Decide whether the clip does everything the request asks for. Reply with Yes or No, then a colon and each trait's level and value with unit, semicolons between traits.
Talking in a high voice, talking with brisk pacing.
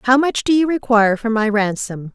Yes: high, 230 Hz; fast, 225 wpm